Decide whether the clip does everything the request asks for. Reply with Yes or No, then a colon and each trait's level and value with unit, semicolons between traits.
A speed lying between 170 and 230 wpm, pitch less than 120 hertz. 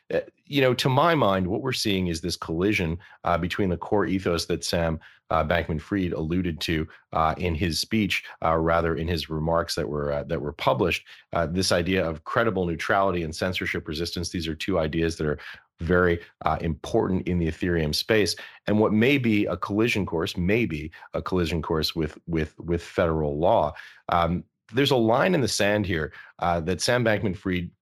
Yes: average, 190 wpm; very low, 85 Hz